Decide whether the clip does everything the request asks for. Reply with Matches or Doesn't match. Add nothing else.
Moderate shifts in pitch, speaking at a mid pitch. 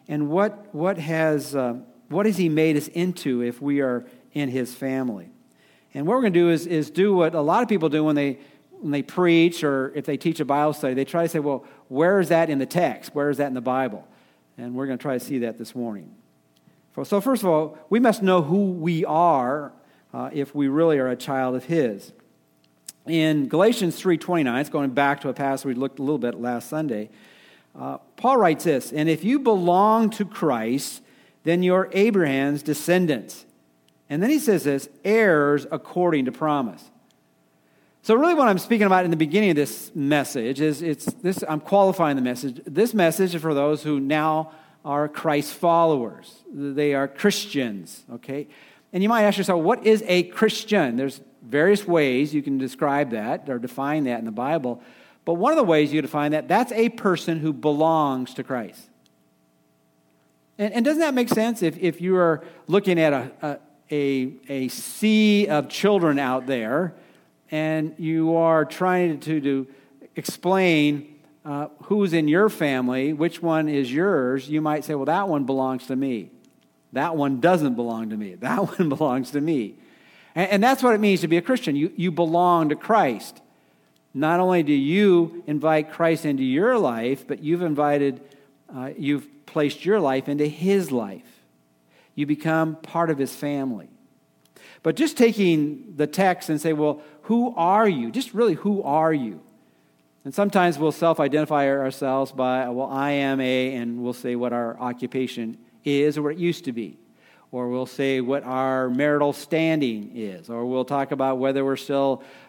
Matches